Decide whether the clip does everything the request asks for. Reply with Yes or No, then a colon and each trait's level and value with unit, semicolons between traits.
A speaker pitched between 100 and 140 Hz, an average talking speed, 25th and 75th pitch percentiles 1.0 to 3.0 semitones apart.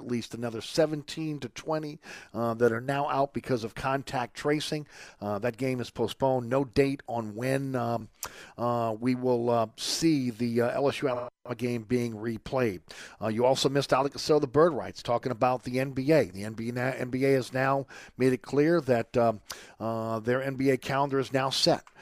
Yes: low, 125 Hz; average, 175 wpm; narrow, 2.6 semitones